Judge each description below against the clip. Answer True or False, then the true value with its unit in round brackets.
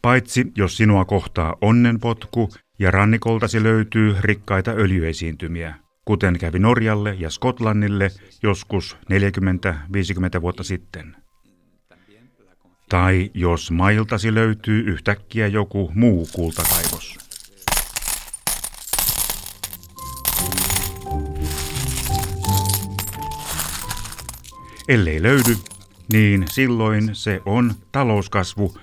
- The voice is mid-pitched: False (100 Hz)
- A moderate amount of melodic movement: True (3.4 semitones)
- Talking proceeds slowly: True (70 wpm)